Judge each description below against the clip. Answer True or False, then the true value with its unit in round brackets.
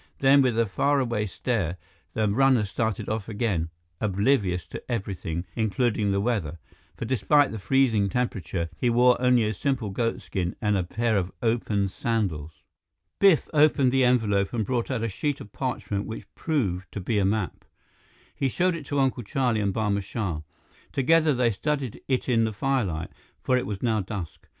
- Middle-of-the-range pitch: False (110 Hz)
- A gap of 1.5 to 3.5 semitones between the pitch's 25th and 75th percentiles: False (4.5 semitones)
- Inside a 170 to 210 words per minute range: True (175 wpm)